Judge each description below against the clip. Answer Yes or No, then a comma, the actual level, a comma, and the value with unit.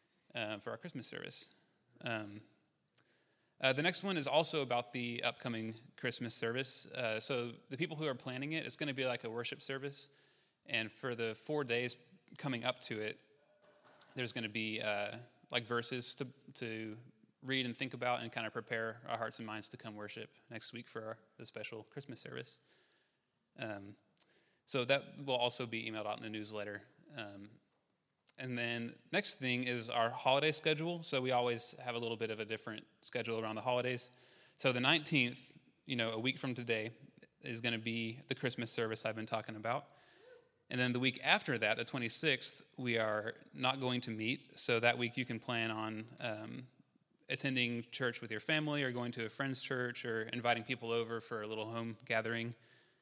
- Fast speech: No, average, 190 wpm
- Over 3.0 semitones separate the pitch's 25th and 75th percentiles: No, narrow, 2.5 semitones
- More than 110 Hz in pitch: Yes, low, 120 Hz